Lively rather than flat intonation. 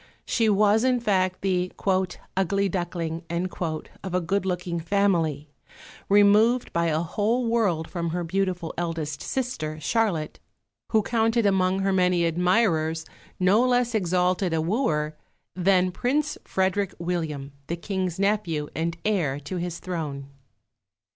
No: average, 3.6 semitones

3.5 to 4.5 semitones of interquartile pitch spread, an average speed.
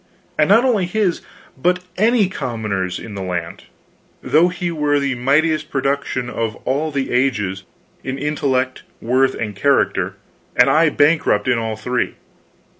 No: average, 5.3 semitones; average, 145 wpm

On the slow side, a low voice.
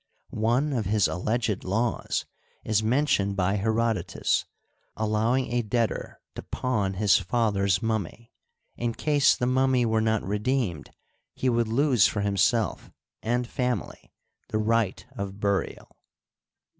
Yes: slow, 130 wpm; low, 110 Hz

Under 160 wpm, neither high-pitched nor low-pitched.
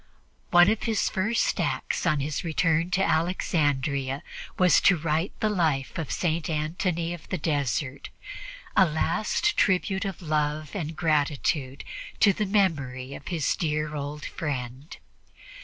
Yes: average, 140 wpm; medium, 160 Hz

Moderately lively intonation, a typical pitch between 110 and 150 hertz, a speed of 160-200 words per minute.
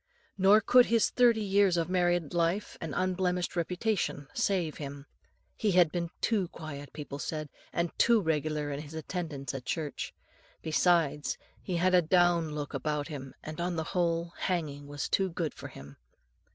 No: average, 3.5 semitones; medium, 170 Hz; average, 165 wpm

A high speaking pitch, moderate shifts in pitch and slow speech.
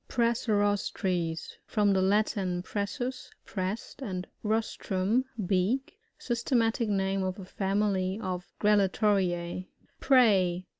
Yes: high, 200 Hz; average, 3.1 semitones; slow, 100 wpm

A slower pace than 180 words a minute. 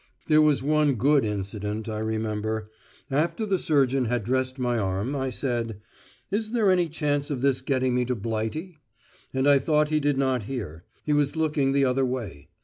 No: average, 185 wpm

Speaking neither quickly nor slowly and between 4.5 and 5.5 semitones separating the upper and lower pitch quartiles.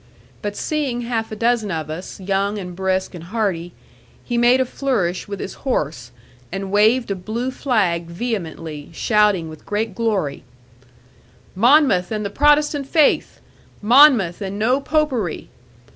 Yes: average, 145 wpm; average, 5.2 semitones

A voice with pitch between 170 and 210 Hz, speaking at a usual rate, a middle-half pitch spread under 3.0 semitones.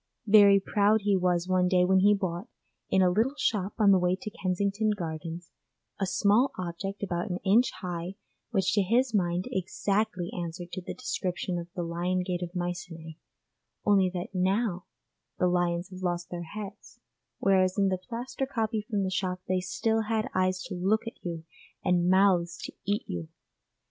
Yes: medium, 185 Hz; average, 180 wpm; narrow, 2.5 semitones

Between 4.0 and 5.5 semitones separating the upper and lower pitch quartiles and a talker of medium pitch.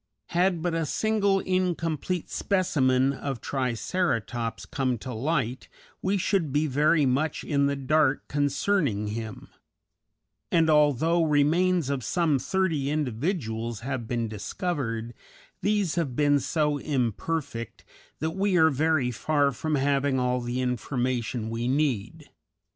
Yes: average, 4.7 semitones; medium, 145 Hz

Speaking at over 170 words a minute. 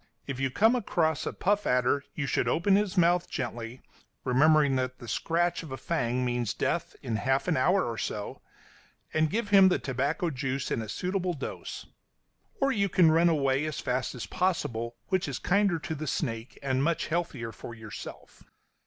Yes: average, 185 wpm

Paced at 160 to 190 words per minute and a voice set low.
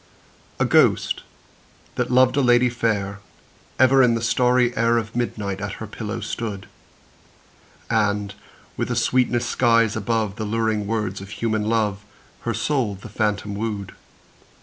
No: average, 145 wpm; low, 110 Hz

